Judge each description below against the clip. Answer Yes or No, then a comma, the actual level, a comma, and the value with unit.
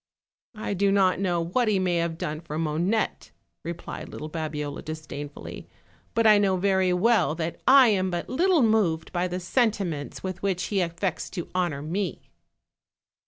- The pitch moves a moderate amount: Yes, average, 3.7 semitones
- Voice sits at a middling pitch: Yes, medium, 180 Hz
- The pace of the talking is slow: No, average, 165 wpm